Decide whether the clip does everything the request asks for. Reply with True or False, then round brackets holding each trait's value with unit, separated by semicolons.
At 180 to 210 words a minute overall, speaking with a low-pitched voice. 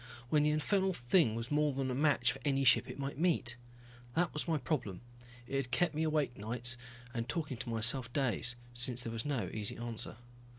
True (205 wpm; 130 Hz)